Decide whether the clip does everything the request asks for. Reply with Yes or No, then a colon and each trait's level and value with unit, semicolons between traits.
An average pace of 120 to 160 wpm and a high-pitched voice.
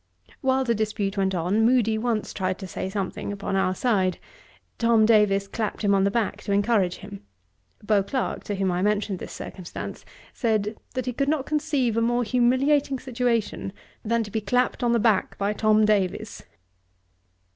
No: average, 175 wpm; high, 215 Hz